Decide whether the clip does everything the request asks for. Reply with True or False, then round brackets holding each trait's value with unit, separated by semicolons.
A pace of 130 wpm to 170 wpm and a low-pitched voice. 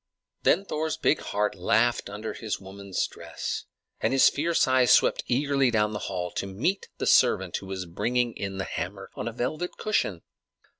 False (180 wpm; 110 Hz)